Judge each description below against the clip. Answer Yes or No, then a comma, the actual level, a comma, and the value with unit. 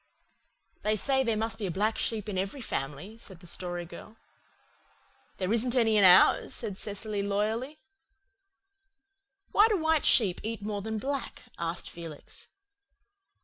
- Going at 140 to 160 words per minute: Yes, average, 145 wpm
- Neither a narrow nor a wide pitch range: Yes, average, 3.4 semitones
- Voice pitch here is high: Yes, high, 215 Hz